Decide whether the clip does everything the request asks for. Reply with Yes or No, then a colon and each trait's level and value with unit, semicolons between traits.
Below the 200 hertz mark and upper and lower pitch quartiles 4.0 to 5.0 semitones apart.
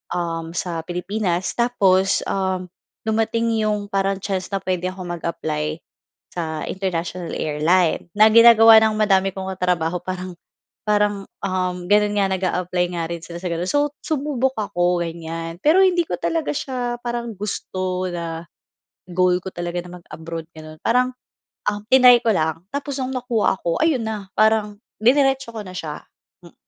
Yes: high, 190 Hz; average, 4.3 semitones